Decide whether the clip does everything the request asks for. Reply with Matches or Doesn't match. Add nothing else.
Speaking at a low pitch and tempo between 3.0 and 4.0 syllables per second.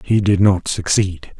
Matches